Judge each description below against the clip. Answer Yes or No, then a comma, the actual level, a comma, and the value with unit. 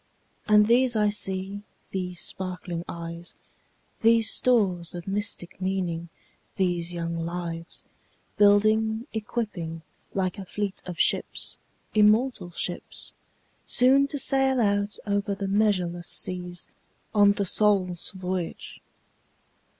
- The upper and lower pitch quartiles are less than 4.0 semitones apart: Yes, average, 3.2 semitones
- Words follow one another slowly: Yes, slow, 110 wpm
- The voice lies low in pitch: No, high, 195 Hz